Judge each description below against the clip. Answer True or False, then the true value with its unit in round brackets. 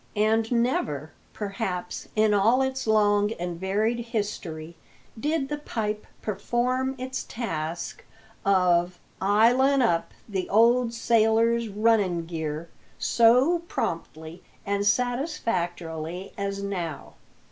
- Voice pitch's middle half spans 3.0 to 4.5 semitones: False (5.0 semitones)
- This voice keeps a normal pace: False (105 wpm)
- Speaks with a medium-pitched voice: False (210 Hz)